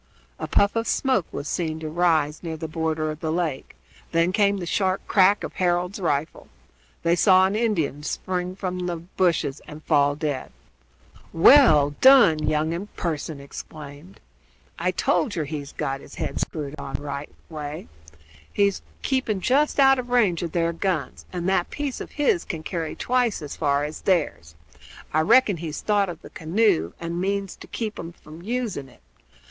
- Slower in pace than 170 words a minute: No, average, 175 wpm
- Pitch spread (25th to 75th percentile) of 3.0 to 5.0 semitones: Yes, average, 4.6 semitones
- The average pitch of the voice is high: No, medium, 170 Hz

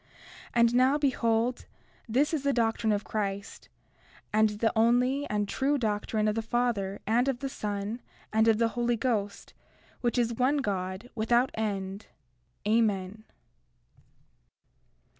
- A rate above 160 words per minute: No, slow, 135 wpm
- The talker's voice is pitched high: Yes, high, 225 Hz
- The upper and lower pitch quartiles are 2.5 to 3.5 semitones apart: Yes, average, 2.8 semitones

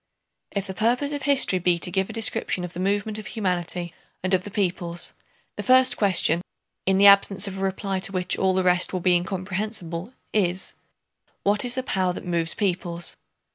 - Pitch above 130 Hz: Yes, high, 190 Hz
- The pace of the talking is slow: No, average, 185 wpm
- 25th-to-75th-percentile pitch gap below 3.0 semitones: Yes, narrow, 2.4 semitones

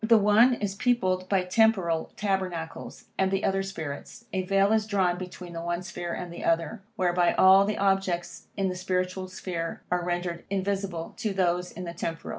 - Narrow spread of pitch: Yes, narrow, 2.1 semitones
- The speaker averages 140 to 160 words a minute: No, average, 190 wpm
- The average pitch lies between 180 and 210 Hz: Yes, medium, 185 Hz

